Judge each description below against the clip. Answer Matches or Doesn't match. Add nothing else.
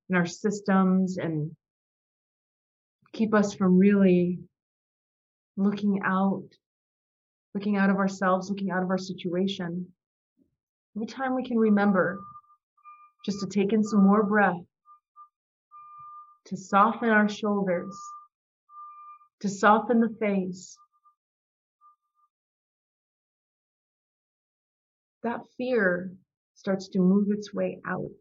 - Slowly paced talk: Matches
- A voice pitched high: Matches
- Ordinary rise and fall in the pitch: Doesn't match